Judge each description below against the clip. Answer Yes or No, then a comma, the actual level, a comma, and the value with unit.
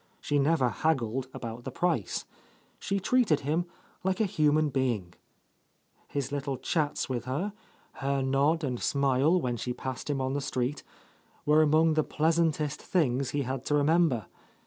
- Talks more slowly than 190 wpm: Yes, average, 155 wpm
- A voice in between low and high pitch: Yes, medium, 145 Hz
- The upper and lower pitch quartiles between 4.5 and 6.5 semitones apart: No, average, 3.3 semitones